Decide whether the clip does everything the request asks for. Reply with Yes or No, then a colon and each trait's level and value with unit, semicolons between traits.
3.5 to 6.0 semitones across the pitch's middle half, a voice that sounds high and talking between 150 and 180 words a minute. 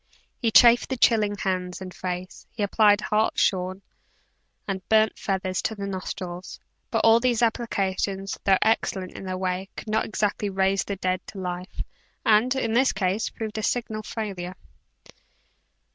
No: average, 2.9 semitones; high, 200 Hz; average, 155 wpm